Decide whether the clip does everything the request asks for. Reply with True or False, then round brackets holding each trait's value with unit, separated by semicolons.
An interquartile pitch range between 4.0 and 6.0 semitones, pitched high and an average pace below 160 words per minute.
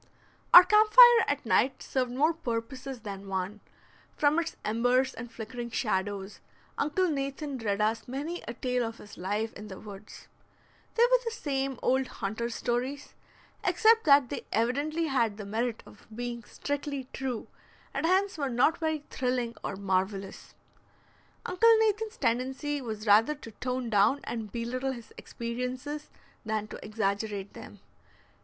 True (4.8 semitones; 250 Hz; 150 wpm)